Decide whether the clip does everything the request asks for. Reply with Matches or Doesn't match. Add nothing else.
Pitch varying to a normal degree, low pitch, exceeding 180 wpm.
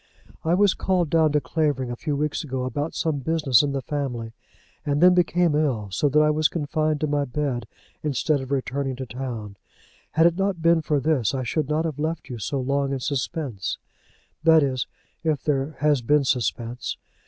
Doesn't match